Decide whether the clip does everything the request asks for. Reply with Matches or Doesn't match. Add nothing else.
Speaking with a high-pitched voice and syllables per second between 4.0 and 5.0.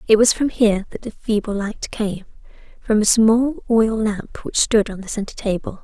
Matches